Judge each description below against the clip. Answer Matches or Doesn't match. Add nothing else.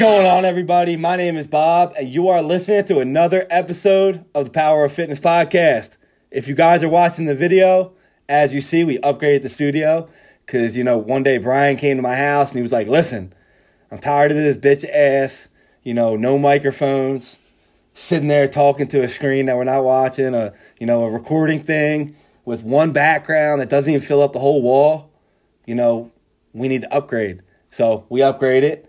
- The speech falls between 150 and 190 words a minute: Doesn't match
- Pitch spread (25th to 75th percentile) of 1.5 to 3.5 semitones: Doesn't match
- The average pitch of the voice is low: Doesn't match